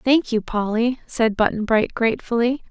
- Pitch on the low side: No, high, 230 Hz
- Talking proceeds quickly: No, average, 155 wpm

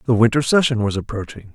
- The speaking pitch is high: No, low, 120 Hz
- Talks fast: No, average, 195 wpm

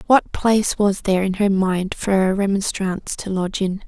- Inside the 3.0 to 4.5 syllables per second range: No, 5.2 syllables/s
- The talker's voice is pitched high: Yes, high, 195 Hz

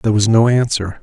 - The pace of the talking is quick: Yes, fast, 235 wpm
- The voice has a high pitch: No, low, 110 Hz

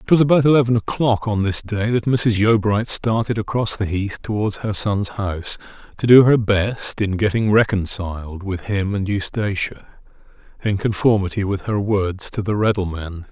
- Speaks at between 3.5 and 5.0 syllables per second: Yes, 4.8 syllables/s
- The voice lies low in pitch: Yes, low, 105 Hz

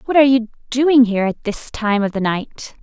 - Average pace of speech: No, fast, 235 wpm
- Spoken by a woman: Yes, female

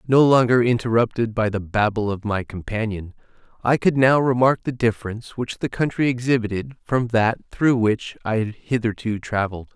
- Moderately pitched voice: No, low, 115 Hz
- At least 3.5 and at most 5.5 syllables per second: Yes, 5.2 syllables/s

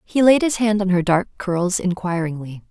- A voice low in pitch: No, high, 190 Hz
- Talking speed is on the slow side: No, average, 200 wpm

